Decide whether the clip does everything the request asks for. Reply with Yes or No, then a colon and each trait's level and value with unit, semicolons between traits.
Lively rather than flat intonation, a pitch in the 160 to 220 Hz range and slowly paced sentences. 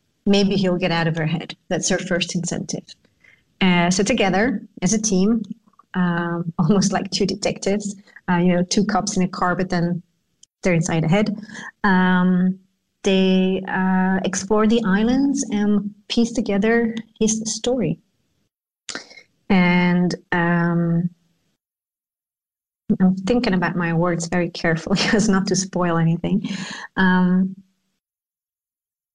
No: average, 2.8 semitones; high, 190 Hz; slow, 130 wpm